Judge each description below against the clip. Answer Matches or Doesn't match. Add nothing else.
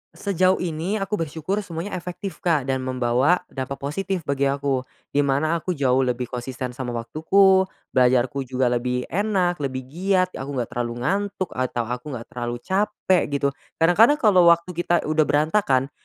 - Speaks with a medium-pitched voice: Matches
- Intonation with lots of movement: Matches